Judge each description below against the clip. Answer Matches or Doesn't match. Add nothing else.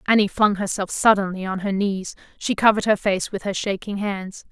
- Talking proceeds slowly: Doesn't match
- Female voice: Matches